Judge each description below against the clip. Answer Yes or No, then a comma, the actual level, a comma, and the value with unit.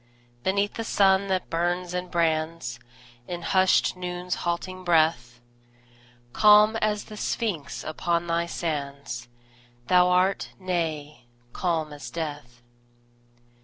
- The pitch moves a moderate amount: Yes, average, 3.0 semitones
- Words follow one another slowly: Yes, slow, 110 wpm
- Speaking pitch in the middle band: Yes, medium, 175 Hz